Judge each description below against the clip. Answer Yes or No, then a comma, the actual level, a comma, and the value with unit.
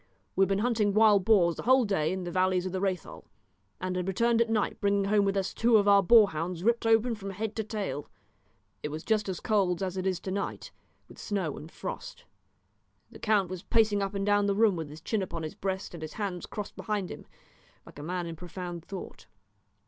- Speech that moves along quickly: Yes, fast, 230 wpm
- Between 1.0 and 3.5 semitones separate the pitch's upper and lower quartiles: Yes, average, 2.8 semitones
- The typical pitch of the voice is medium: No, high, 195 Hz